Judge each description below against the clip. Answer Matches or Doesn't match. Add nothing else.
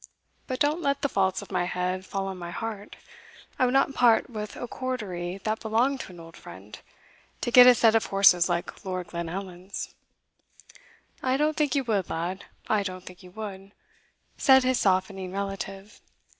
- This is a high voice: Matches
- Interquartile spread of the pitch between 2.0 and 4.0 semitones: Doesn't match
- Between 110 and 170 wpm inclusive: Doesn't match